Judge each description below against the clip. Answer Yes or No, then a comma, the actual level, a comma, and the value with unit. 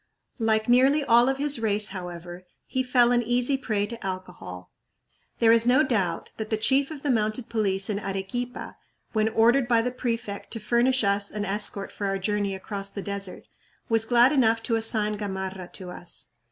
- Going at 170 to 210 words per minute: Yes, average, 185 wpm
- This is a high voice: Yes, high, 220 Hz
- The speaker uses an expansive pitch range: No, average, 3.5 semitones